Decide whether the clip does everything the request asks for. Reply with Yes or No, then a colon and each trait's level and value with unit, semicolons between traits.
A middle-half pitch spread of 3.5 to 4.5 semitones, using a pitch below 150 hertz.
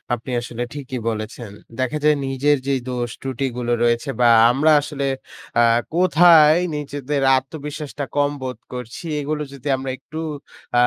No: average, 3.1 semitones; low, 135 Hz